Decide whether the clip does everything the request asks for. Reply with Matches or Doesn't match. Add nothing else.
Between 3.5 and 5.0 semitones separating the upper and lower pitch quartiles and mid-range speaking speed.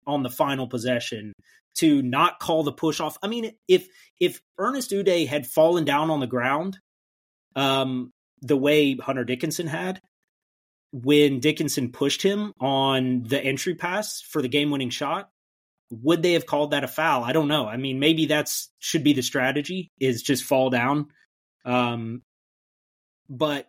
Matches